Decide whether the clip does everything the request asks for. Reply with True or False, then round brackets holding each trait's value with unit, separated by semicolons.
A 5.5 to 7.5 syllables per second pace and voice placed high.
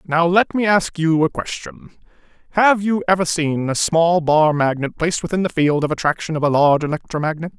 False (5.7 syllables/s; 165 Hz)